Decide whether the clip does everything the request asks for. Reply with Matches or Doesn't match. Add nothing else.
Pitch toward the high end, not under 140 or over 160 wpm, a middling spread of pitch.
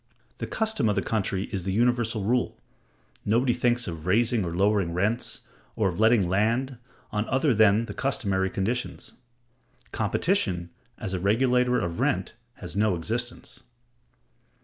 Doesn't match